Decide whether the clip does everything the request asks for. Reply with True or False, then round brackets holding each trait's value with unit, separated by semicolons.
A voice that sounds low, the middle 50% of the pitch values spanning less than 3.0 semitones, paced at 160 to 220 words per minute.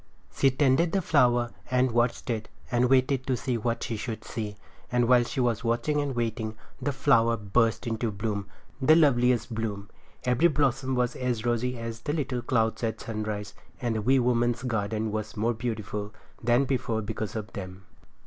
True (120 Hz; 2.4 semitones; 175 wpm)